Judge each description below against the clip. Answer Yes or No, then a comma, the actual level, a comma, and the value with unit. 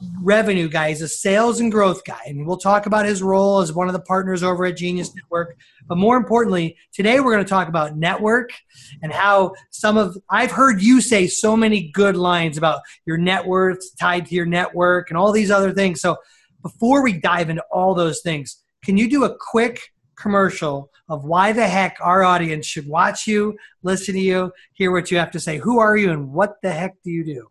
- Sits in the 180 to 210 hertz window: Yes, medium, 185 Hz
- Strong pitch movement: No, average, 3.3 semitones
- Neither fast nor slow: No, fast, 220 wpm